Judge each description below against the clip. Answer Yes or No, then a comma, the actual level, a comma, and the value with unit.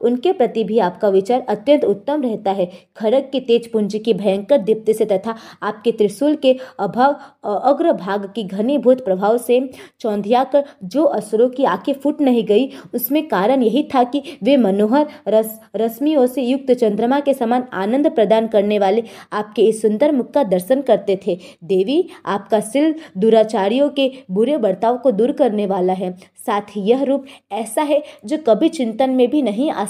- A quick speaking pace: No, average, 175 wpm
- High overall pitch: Yes, high, 235 Hz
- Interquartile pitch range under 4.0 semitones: No, average, 4.7 semitones